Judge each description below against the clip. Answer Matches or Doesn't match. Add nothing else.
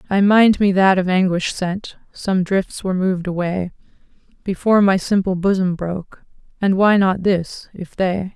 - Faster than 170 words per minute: Doesn't match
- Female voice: Matches